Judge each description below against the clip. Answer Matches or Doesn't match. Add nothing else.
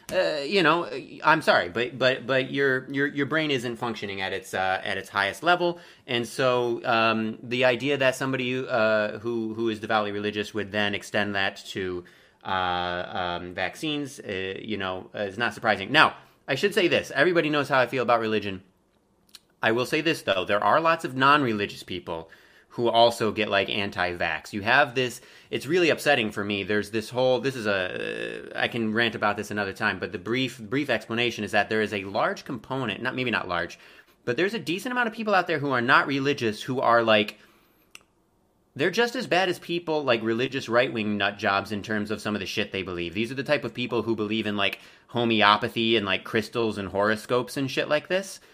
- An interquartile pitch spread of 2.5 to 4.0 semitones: Doesn't match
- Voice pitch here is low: Matches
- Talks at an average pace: Doesn't match